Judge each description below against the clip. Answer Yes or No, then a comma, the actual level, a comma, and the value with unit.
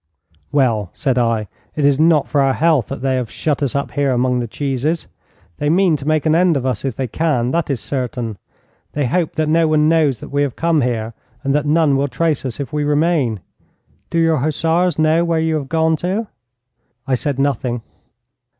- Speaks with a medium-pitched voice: Yes, medium, 145 Hz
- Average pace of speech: No, fast, 210 wpm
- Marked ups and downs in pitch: No, average, 3.7 semitones